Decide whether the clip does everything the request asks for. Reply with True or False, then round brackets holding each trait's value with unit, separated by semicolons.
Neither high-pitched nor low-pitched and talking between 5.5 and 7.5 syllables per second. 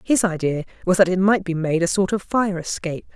True (180 Hz; 5.8 syllables/s)